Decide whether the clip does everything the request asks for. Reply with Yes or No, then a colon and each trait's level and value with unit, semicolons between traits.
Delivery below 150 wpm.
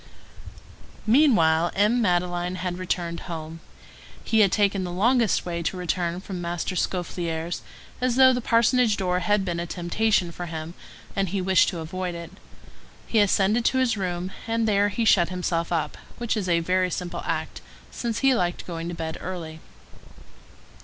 No: average, 175 wpm